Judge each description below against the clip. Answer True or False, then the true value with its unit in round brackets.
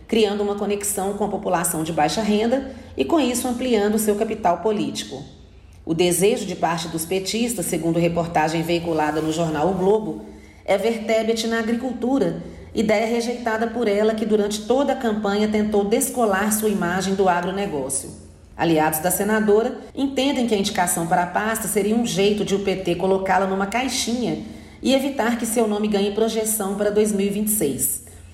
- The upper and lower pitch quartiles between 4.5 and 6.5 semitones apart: False (3.9 semitones)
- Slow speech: False (160 wpm)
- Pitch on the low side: False (205 Hz)